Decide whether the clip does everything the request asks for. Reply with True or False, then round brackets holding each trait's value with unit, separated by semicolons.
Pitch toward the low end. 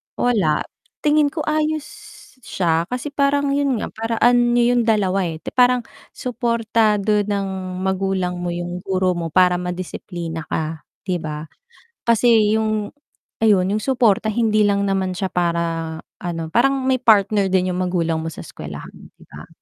False (205 Hz)